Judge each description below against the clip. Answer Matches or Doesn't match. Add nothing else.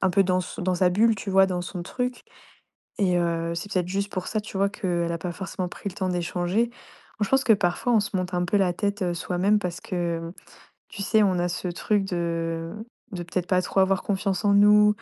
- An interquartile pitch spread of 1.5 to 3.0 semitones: Matches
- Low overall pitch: Doesn't match